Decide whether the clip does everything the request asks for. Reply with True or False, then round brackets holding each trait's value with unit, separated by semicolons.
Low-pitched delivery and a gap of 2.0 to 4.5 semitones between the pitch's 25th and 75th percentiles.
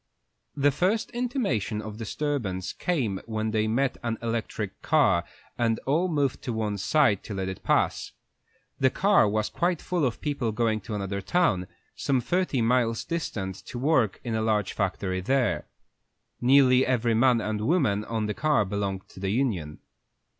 False (115 Hz; 5.0 semitones)